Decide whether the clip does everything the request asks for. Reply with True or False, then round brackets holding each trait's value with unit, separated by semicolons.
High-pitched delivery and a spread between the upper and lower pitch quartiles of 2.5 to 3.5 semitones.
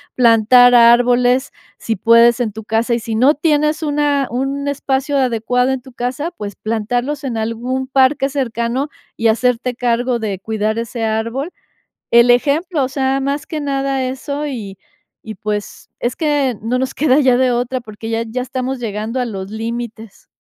True (245 Hz; 2.9 semitones)